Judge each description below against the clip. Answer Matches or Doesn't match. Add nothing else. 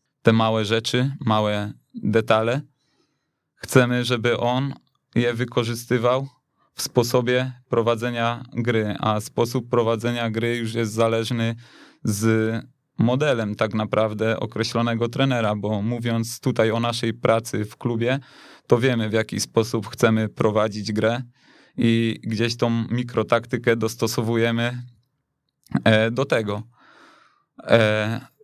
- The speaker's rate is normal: Doesn't match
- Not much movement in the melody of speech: Matches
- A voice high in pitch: Doesn't match